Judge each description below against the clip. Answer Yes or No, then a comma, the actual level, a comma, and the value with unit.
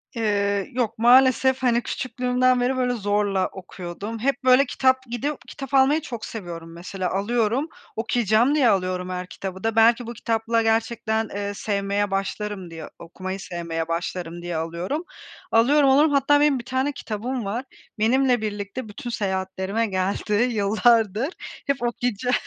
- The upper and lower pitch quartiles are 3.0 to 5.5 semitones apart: Yes, average, 4.4 semitones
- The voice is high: Yes, high, 225 Hz